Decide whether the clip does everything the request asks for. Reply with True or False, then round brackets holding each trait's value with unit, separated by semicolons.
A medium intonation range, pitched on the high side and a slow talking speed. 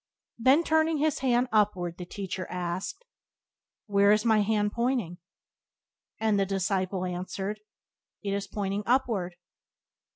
True (4.1 semitones; 205 Hz; 130 wpm)